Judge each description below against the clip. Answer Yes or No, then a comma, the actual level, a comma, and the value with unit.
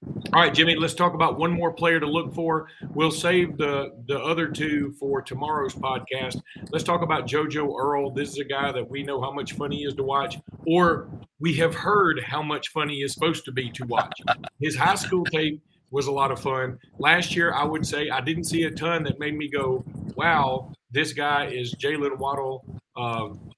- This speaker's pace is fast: Yes, fast, 215 wpm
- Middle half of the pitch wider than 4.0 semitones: No, average, 3.1 semitones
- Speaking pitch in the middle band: Yes, medium, 150 Hz